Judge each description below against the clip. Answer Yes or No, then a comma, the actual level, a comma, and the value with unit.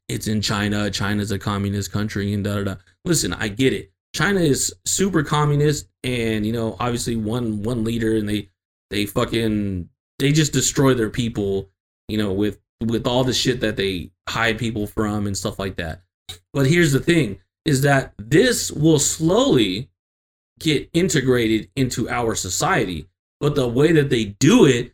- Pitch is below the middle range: Yes, low, 110 Hz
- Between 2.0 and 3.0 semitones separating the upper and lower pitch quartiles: No, average, 4.8 semitones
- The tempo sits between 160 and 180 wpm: Yes, average, 175 wpm